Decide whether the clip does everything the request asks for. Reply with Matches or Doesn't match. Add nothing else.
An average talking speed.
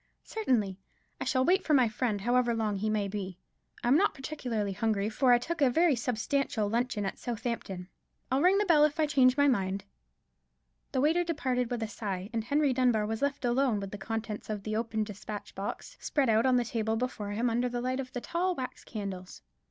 Doesn't match